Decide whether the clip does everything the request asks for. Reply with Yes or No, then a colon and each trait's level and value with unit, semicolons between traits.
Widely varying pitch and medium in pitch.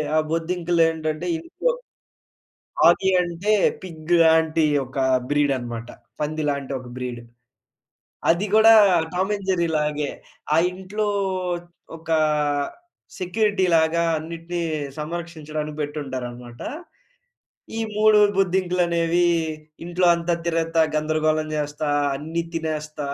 No: narrow, 2.5 semitones; medium, 165 Hz